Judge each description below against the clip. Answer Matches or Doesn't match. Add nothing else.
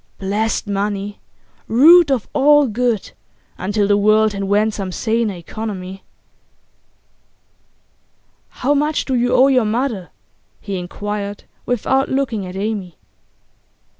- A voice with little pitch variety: Doesn't match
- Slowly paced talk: Matches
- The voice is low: Doesn't match